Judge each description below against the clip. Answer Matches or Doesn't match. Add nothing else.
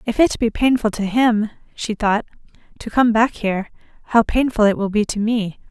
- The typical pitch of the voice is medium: Doesn't match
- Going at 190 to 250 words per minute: Matches